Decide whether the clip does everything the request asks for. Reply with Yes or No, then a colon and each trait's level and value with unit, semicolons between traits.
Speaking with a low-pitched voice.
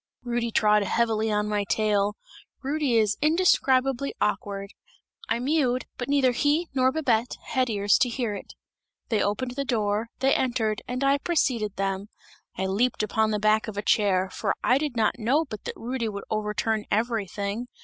No: high, 225 Hz